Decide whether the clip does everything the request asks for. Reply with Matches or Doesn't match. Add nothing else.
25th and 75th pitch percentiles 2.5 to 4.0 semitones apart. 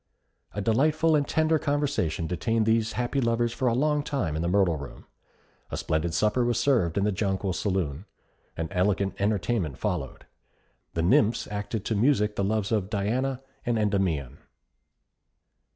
Doesn't match